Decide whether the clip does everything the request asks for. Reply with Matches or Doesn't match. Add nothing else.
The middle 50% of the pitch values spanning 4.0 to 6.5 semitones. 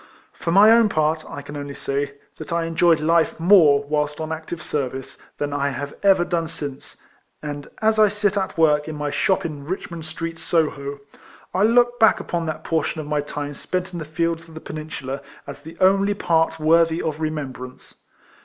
Doesn't match